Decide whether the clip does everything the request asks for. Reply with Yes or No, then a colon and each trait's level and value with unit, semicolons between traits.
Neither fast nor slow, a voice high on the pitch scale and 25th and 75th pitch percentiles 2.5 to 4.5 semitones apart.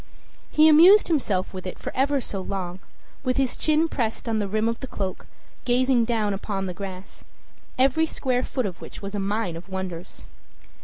No: average, 190 wpm; high, 220 Hz; wide, 5.5 semitones